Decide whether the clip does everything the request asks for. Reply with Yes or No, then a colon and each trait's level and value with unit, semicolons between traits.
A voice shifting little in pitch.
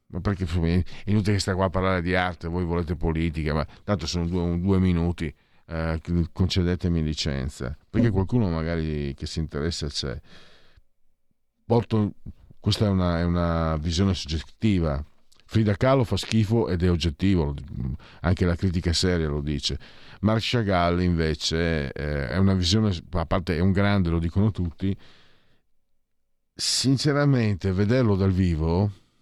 No: average, 3.6 semitones